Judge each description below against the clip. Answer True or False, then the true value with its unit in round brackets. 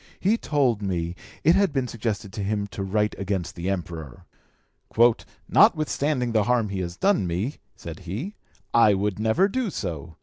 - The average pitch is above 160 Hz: False (105 Hz)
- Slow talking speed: False (165 wpm)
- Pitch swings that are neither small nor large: False (6.2 semitones)